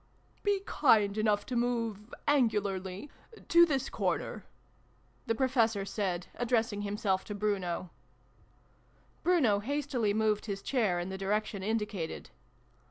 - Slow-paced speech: Yes, slow, 125 wpm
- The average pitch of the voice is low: No, high, 215 Hz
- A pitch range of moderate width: Yes, average, 3.4 semitones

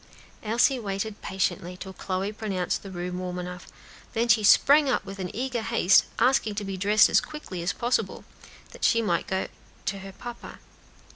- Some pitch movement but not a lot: Yes, average, 3.7 semitones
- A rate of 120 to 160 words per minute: No, average, 170 wpm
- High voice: Yes, high, 200 Hz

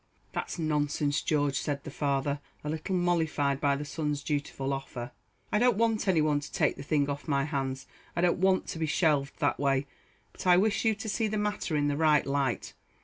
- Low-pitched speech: No, medium, 150 Hz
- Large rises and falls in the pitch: No, average, 3.9 semitones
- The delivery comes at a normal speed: No, fast, 210 wpm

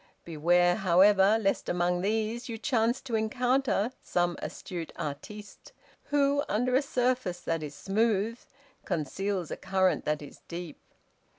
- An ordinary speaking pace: No, slow, 130 wpm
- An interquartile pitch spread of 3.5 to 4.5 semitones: No, average, 5.0 semitones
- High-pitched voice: Yes, high, 200 Hz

